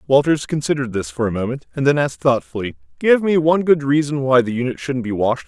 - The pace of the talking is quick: Yes, fast, 240 wpm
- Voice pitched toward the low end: Yes, low, 130 Hz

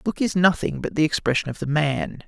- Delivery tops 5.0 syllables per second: Yes, 6.3 syllables/s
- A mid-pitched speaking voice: Yes, medium, 150 Hz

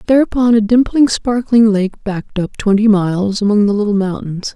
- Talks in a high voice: Yes, high, 210 Hz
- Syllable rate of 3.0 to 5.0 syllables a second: No, 5.4 syllables/s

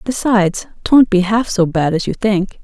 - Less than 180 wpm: No, fast, 205 wpm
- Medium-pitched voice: No, high, 205 Hz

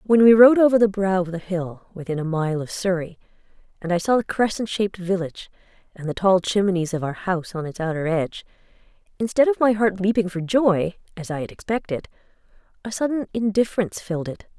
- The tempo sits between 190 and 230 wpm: Yes, average, 195 wpm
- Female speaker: Yes, female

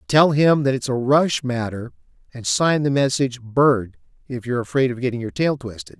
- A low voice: Yes, low, 130 Hz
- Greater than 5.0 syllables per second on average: Yes, 5.5 syllables/s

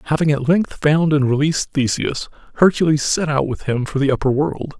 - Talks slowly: No, average, 200 wpm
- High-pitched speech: No, medium, 150 Hz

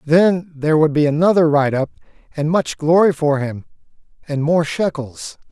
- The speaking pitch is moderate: Yes, medium, 155 Hz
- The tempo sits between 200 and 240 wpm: No, average, 165 wpm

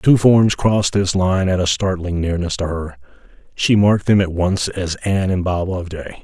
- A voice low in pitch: Yes, very low, 90 Hz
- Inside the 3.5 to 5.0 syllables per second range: No, 5.2 syllables/s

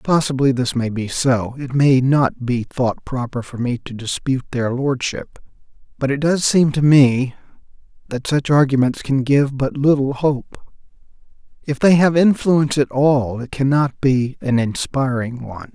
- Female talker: No, male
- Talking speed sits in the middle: Yes, average, 165 wpm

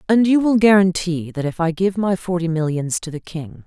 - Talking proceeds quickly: Yes, fast, 230 wpm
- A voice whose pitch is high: No, medium, 180 Hz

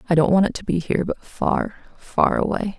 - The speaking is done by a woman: Yes, female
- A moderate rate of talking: No, fast, 235 wpm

